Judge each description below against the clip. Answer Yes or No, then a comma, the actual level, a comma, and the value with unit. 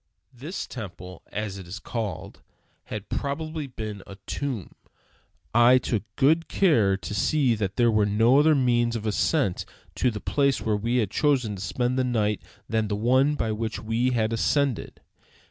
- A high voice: No, low, 115 Hz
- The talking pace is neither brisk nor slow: Yes, average, 170 wpm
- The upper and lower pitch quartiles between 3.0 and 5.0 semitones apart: Yes, average, 4.0 semitones